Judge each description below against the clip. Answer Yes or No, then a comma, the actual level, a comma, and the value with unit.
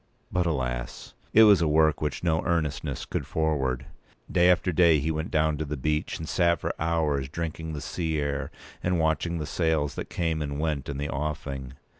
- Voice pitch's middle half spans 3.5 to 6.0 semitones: No, narrow, 2.5 semitones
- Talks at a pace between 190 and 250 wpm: Yes, average, 195 wpm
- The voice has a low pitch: Yes, very low, 80 Hz